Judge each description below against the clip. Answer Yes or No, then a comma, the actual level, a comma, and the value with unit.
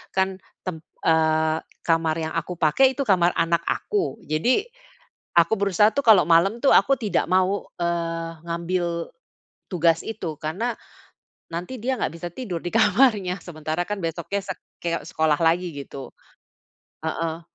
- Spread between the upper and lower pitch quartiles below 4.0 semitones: Yes, average, 3.5 semitones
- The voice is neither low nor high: Yes, medium, 175 Hz